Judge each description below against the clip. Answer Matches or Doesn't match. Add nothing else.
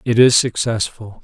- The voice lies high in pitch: Doesn't match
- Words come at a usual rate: Matches